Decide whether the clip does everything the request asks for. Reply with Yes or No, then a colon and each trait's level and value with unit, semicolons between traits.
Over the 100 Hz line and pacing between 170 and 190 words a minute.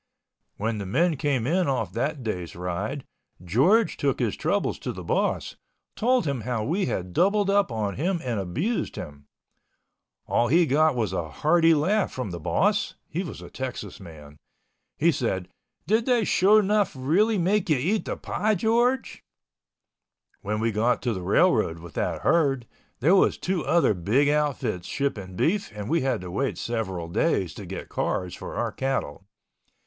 Yes: low, 135 Hz; average, 175 wpm